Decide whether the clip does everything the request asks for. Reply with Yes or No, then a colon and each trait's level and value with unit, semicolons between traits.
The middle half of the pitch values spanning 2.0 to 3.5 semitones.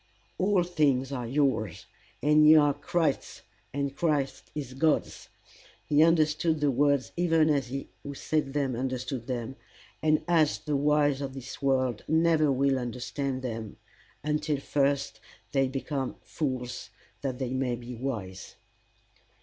Yes: average, 2.7 semitones